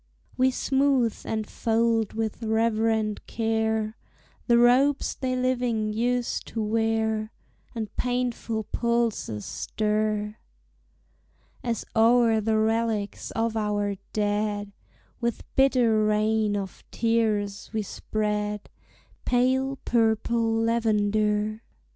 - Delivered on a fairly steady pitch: Yes, narrow, 1.7 semitones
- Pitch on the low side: No, high, 220 Hz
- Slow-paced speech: Yes, slow, 95 wpm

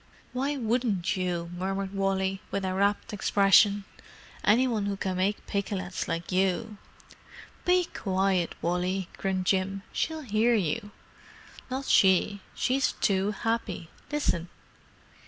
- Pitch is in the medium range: No, high, 195 Hz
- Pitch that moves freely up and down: No, average, 2.8 semitones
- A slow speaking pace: Yes, slow, 120 wpm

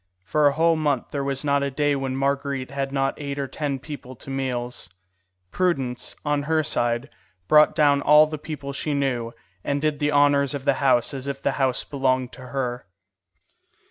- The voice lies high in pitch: No, medium, 140 Hz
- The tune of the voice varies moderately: No, narrow, 1.8 semitones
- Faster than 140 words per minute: Yes, average, 190 wpm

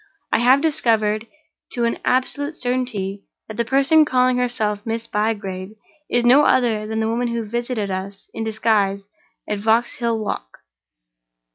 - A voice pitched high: Yes, high, 225 Hz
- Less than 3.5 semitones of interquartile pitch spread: Yes, average, 2.9 semitones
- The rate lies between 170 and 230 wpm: No, average, 145 wpm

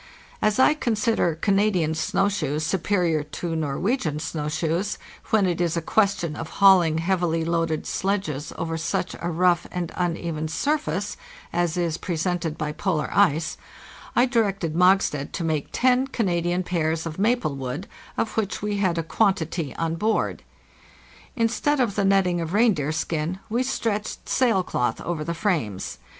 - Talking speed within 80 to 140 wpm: No, average, 155 wpm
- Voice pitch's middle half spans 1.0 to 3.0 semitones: No, average, 4.2 semitones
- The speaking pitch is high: No, medium, 175 Hz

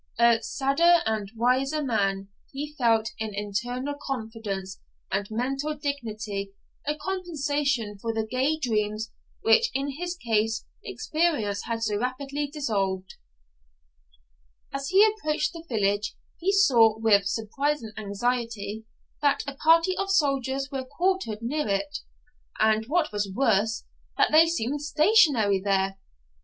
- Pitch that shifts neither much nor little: No, wide, 5.7 semitones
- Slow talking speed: Yes, slow, 130 wpm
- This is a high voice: Yes, high, 245 Hz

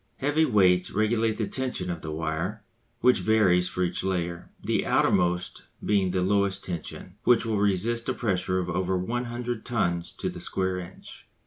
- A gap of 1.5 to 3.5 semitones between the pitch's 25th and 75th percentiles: No, average, 3.9 semitones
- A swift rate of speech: No, average, 175 wpm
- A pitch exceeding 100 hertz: No, very low, 95 Hz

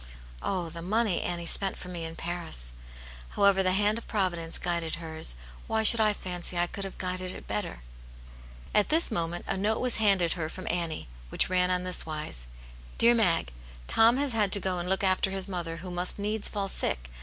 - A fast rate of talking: Yes, fast, 210 wpm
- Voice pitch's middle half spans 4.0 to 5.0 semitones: No, average, 3.2 semitones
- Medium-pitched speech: Yes, medium, 180 Hz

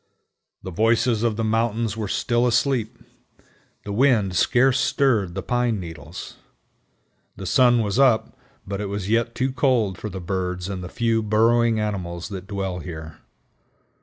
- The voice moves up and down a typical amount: Yes, average, 3.8 semitones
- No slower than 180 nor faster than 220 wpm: No, average, 155 wpm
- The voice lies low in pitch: Yes, low, 110 Hz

